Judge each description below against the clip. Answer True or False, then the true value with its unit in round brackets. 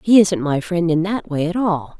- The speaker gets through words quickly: True (270 wpm)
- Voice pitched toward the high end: False (175 Hz)